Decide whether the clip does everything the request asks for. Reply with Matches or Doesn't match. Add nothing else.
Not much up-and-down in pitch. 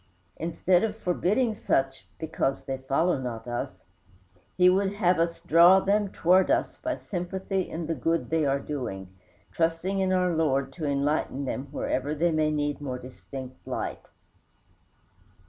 Doesn't match